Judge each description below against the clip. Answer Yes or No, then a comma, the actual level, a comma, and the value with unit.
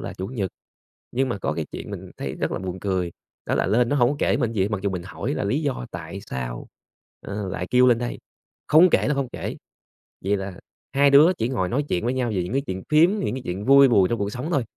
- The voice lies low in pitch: Yes, low, 115 Hz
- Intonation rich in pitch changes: Yes, wide, 6.2 semitones